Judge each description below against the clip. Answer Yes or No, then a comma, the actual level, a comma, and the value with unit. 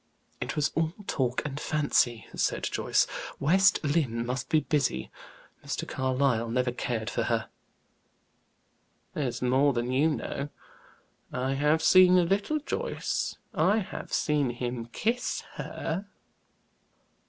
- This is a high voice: No, medium, 140 Hz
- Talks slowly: Yes, slow, 125 wpm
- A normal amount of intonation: Yes, average, 4.7 semitones